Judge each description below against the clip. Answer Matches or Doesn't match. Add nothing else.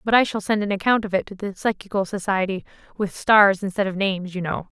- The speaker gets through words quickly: Matches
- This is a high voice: Matches